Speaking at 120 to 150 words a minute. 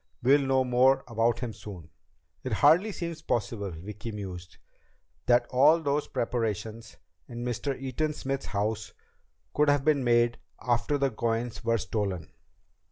Yes: average, 140 wpm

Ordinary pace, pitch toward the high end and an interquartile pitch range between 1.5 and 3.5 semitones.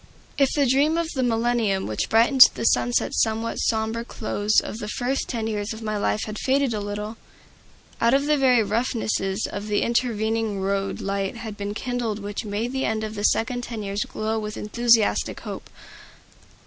Yes: average, 180 wpm; high, 220 Hz; average, 2.7 semitones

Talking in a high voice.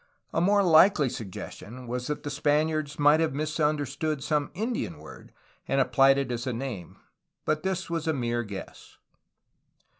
No: medium, 145 Hz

